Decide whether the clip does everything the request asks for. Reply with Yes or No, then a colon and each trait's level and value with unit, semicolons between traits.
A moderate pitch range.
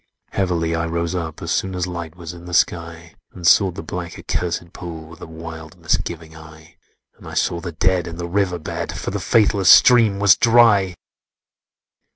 No: narrow, 2.1 semitones